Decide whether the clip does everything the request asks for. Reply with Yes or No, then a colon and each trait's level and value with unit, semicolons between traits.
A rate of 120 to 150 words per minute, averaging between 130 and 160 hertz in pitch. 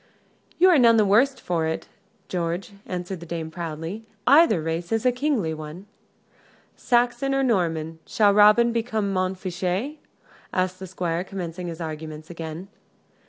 No: average, 140 wpm; medium, 185 Hz